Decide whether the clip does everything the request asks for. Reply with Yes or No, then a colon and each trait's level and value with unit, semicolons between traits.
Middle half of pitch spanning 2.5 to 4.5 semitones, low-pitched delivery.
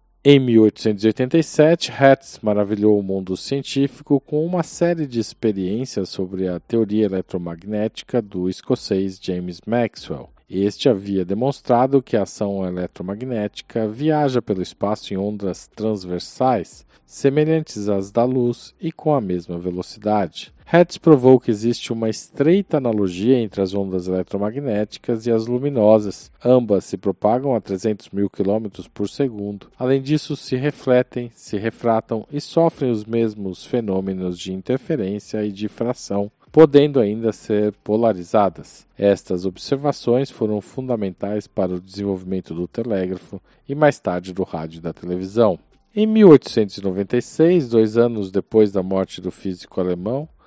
No: average, 5.2 semitones; low, 110 Hz